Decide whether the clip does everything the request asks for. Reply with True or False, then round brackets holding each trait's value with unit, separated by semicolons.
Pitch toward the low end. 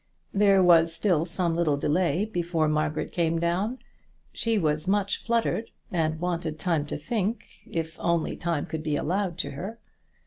False (170 Hz)